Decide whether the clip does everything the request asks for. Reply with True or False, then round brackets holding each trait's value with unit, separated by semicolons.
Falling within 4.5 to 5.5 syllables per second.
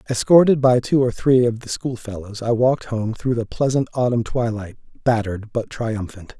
True (5.1 syllables/s)